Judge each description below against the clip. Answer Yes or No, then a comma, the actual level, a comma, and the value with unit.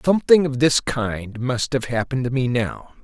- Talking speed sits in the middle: Yes, average, 195 wpm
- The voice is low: Yes, low, 130 Hz